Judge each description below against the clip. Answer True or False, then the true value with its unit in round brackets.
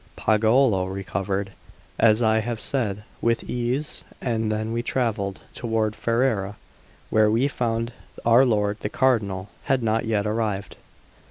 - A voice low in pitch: True (110 Hz)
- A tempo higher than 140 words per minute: False (135 wpm)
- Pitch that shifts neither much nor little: False (2.3 semitones)